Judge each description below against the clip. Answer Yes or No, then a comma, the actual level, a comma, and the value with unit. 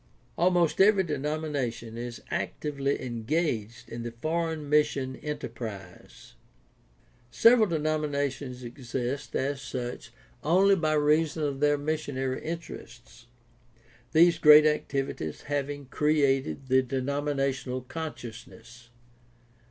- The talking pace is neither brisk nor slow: No, slow, 105 wpm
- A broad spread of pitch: No, average, 3.6 semitones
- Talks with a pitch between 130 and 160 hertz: Yes, medium, 140 Hz